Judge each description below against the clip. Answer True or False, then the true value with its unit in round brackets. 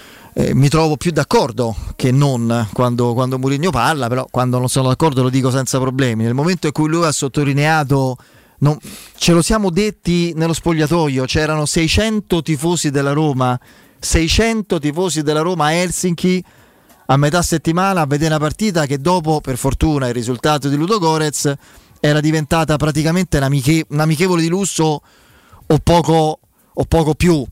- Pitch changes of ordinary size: True (3.8 semitones)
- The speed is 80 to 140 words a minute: False (165 wpm)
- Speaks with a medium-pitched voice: True (155 Hz)